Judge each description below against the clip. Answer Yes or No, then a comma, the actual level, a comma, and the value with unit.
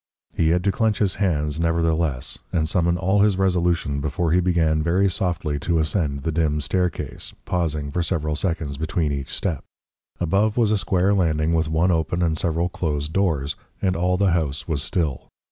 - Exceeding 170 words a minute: Yes, average, 180 wpm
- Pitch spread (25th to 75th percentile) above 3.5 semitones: No, average, 2.9 semitones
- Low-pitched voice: Yes, very low, 85 Hz